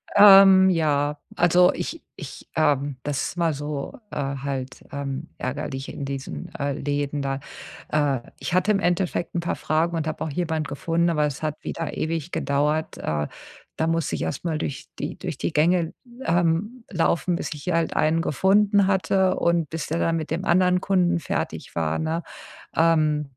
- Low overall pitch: No, medium, 160 Hz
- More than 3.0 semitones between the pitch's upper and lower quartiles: Yes, average, 3.4 semitones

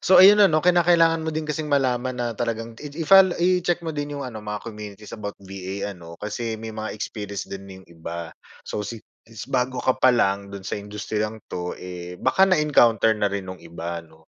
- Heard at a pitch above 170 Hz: No, low, 110 Hz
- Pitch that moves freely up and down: Yes, wide, 6.9 semitones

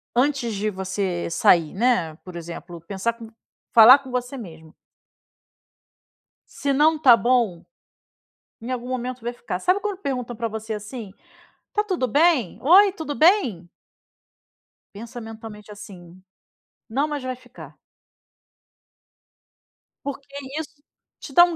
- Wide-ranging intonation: Yes, wide, 5.7 semitones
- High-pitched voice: Yes, high, 240 Hz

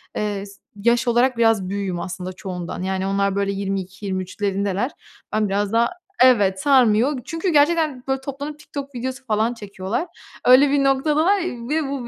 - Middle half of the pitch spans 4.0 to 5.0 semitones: No, wide, 5.5 semitones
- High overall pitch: Yes, high, 225 Hz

